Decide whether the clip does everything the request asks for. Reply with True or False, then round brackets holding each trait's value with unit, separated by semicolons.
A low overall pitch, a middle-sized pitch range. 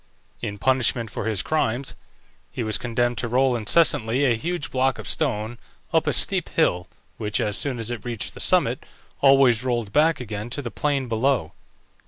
True (120 Hz; 3.3 semitones)